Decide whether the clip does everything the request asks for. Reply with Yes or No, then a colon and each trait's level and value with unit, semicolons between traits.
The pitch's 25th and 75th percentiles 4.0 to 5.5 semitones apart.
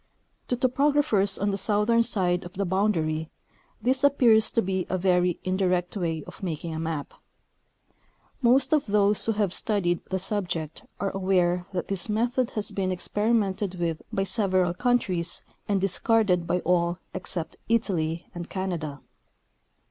No: average, 3.4 semitones